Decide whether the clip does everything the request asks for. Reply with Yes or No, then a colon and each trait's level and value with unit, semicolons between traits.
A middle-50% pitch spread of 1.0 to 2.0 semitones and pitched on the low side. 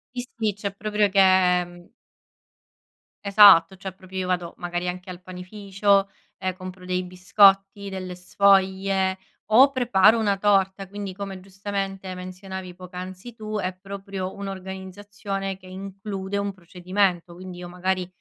No: narrow, 1.4 semitones; high, 190 Hz